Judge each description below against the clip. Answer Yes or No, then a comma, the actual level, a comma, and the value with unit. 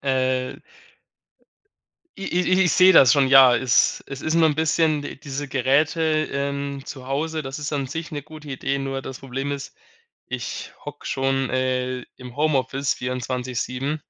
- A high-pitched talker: No, medium, 140 Hz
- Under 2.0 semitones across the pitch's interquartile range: No, average, 2.7 semitones